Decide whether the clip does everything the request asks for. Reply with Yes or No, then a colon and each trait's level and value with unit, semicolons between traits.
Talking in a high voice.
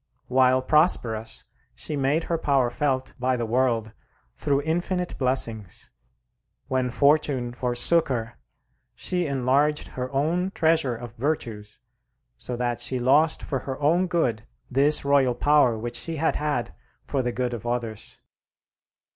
No: low, 130 Hz